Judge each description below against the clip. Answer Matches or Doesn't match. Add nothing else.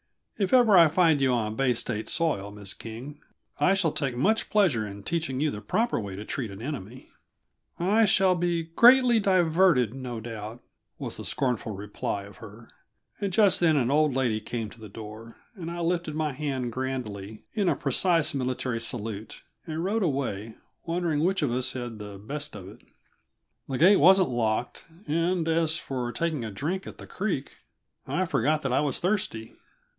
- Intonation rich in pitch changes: Matches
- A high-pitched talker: Doesn't match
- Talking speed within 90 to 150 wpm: Doesn't match